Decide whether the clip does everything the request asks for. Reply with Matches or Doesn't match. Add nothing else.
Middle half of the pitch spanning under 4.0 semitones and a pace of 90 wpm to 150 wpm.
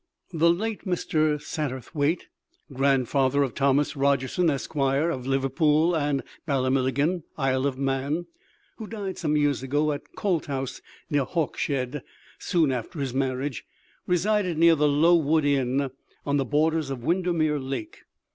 Matches